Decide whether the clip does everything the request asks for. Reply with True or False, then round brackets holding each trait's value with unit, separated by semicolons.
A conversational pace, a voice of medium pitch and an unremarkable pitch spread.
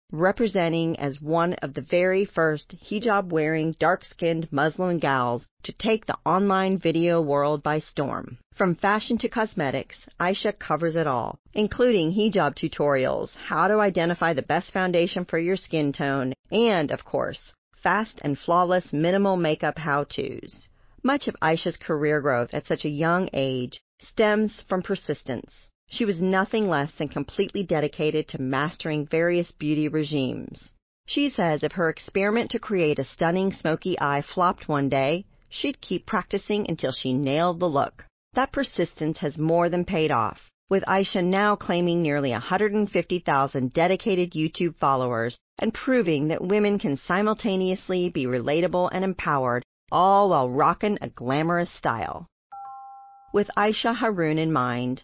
True (145 wpm; 170 Hz; 4.6 semitones)